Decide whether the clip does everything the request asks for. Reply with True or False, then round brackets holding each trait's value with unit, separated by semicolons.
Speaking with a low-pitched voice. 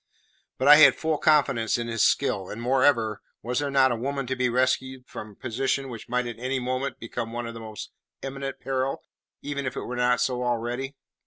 True (125 Hz)